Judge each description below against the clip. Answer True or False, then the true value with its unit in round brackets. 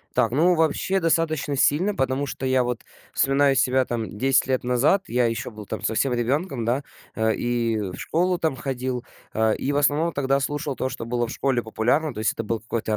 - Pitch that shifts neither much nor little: True (3.7 semitones)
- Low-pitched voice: True (130 Hz)